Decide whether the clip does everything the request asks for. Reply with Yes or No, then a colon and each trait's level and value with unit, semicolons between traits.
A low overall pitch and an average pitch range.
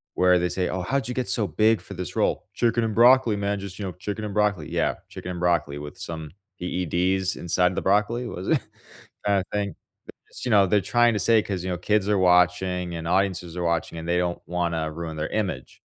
Yes: very low, 90 Hz; average, 3.0 semitones